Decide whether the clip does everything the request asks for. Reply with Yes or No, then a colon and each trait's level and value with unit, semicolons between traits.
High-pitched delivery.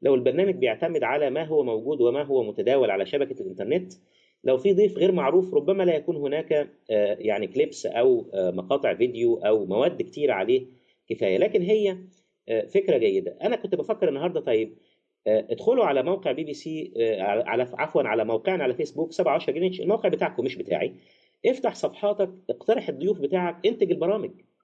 Yes: high, 210 Hz